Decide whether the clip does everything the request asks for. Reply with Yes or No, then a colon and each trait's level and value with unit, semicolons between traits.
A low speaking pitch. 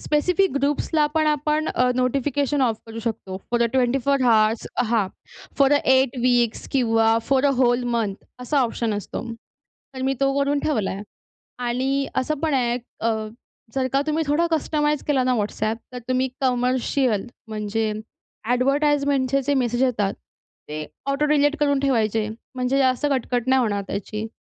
No: very high, 255 Hz